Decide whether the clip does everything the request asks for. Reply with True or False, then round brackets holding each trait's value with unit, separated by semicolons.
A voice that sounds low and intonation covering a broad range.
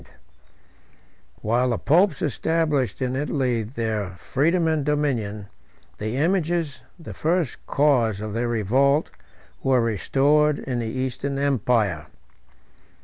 False (130 Hz; 4.7 semitones)